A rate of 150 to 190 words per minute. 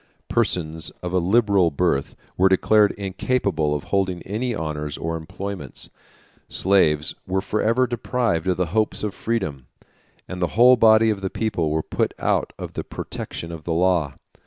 Yes: average, 160 wpm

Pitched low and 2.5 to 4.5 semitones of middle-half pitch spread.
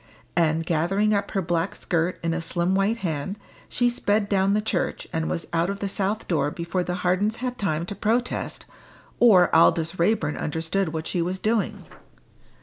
No: medium, 185 Hz; average, 3.6 semitones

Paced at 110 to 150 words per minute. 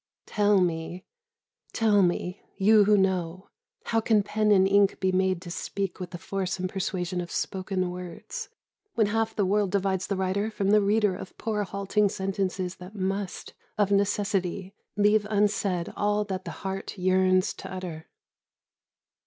No: average, 160 wpm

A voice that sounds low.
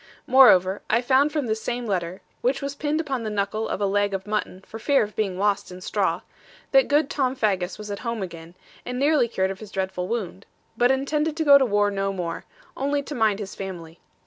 No: high, 215 Hz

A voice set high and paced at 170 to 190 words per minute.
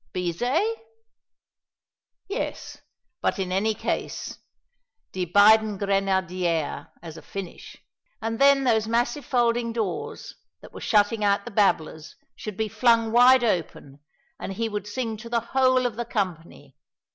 No: high, 215 Hz; slow, 135 wpm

